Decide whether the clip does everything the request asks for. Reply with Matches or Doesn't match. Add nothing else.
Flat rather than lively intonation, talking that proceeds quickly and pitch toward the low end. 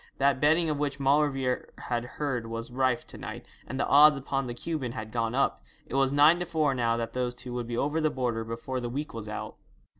Doesn't match